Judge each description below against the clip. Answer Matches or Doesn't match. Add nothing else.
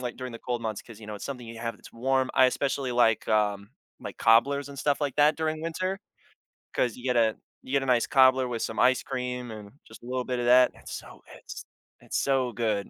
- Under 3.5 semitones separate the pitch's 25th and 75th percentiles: Matches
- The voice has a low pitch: Matches